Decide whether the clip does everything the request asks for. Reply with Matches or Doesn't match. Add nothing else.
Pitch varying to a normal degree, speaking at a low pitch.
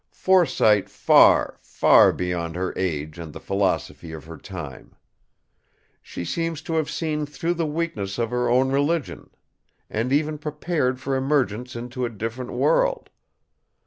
Doesn't match